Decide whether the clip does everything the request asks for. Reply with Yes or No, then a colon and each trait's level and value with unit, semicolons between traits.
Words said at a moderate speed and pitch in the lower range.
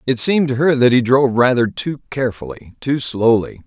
Yes: average, 195 wpm; low, 125 Hz